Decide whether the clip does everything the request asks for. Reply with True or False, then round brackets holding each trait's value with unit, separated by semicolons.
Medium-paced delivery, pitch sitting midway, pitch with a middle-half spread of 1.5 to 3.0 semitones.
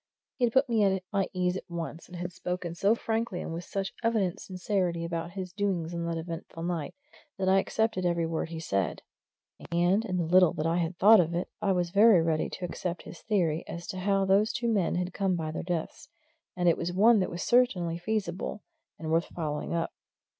False (220 wpm; 180 Hz; 2.7 semitones)